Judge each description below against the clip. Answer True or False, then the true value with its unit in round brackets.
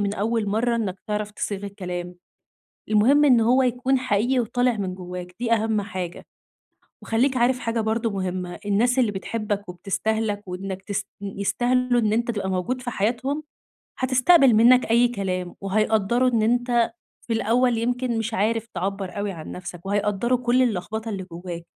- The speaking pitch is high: True (220 Hz)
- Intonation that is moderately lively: True (3.7 semitones)